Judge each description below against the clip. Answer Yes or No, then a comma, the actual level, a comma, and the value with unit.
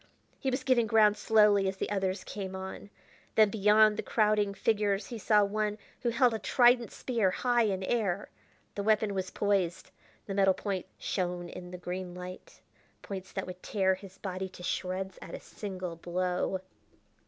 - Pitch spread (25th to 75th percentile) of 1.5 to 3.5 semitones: Yes, narrow, 2.4 semitones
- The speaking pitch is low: No, high, 200 Hz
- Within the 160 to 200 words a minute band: Yes, average, 175 wpm